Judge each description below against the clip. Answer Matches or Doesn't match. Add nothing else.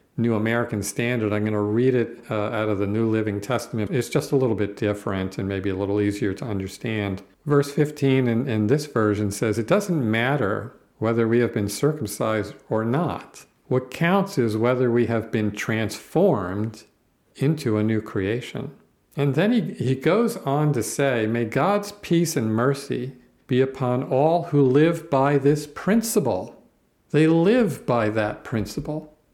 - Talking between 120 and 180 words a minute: Matches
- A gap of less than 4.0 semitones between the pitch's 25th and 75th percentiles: Doesn't match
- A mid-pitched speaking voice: Doesn't match